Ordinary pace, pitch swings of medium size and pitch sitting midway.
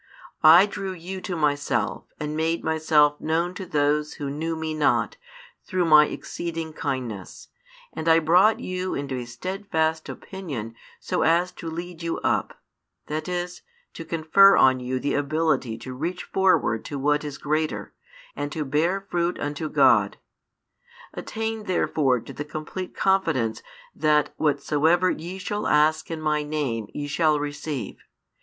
Yes: average, 150 wpm; average, 3.2 semitones; medium, 155 Hz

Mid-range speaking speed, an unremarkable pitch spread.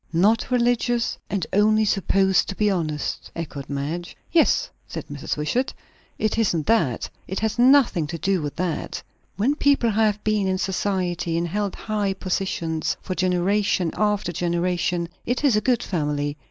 Yes: average, 155 wpm; average, 4.0 semitones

